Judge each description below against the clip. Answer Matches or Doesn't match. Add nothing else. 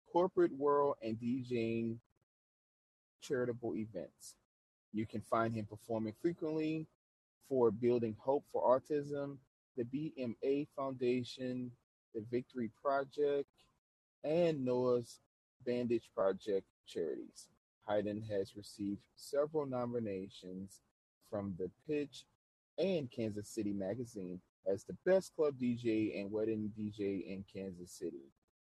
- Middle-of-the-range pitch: Doesn't match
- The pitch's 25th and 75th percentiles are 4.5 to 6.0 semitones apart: Matches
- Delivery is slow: Matches